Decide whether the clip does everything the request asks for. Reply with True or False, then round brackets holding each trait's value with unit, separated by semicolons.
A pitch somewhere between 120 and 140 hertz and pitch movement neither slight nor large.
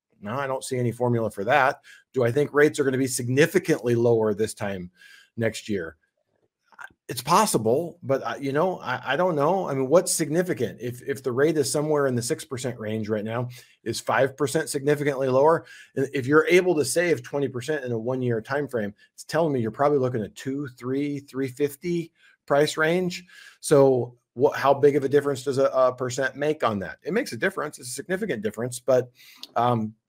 True (135 Hz; 3.5 semitones)